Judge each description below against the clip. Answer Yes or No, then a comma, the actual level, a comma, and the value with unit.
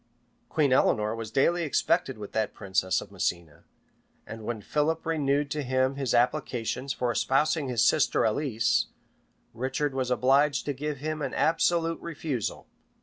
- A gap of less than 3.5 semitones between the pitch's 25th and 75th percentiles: No, average, 4.5 semitones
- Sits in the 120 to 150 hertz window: Yes, low, 135 Hz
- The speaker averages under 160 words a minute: Yes, average, 150 wpm